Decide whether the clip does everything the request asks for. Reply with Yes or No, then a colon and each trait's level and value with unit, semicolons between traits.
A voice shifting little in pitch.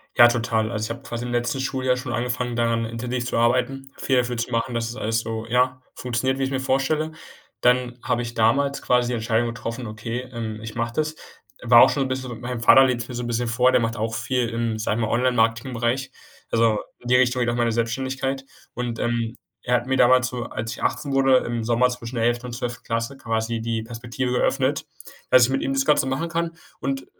Yes: narrow, 1.9 semitones